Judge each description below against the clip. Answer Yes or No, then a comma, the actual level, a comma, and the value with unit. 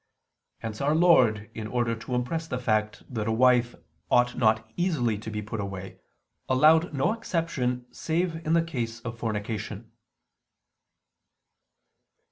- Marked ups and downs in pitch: Yes, wide, 6.1 semitones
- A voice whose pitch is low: Yes, low, 120 Hz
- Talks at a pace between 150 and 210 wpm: No, slow, 135 wpm